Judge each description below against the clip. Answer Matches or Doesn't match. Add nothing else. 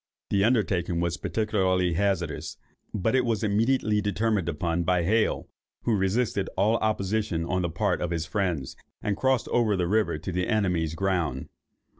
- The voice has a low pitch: Matches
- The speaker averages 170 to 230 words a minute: Doesn't match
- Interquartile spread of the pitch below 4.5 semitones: Matches